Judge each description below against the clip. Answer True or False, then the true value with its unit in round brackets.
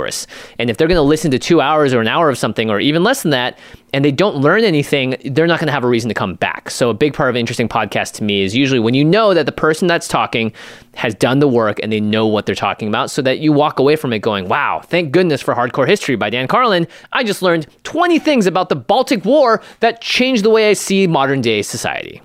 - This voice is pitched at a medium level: True (145 Hz)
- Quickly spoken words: True (270 wpm)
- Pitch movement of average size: False (6.9 semitones)